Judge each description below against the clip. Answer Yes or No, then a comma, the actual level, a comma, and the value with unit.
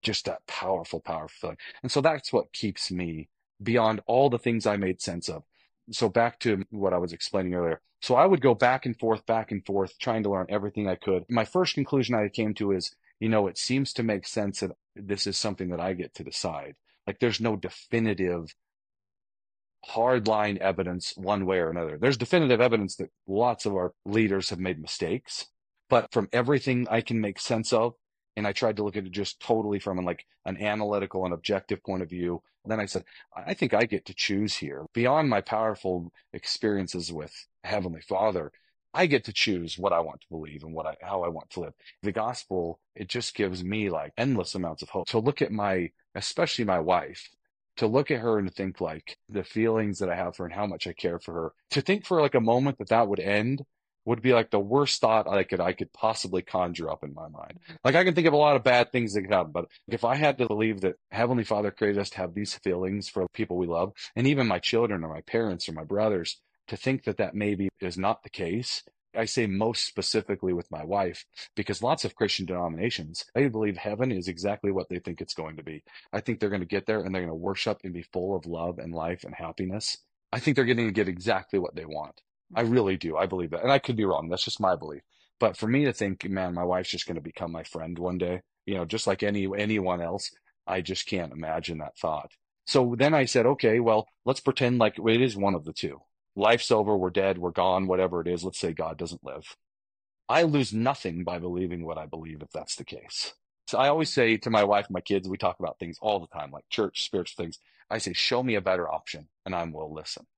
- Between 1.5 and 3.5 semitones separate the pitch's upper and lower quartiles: No, average, 4.0 semitones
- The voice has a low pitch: Yes, low, 100 Hz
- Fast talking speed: Yes, fast, 235 wpm